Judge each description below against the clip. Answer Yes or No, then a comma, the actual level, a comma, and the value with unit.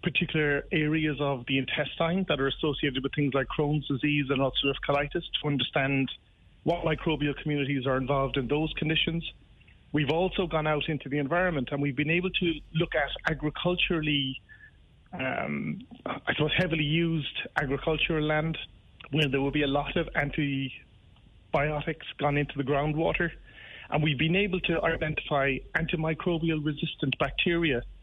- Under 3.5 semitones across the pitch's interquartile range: Yes, average, 2.7 semitones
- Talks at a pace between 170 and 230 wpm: No, average, 150 wpm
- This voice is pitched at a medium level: Yes, medium, 150 Hz